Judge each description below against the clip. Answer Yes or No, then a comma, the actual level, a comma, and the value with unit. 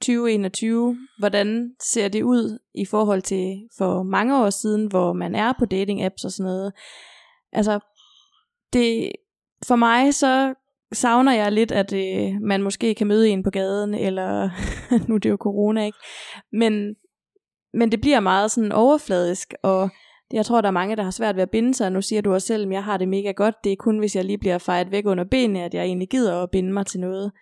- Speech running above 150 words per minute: Yes, average, 210 wpm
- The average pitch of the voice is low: No, high, 210 Hz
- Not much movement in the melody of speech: No, average, 3.4 semitones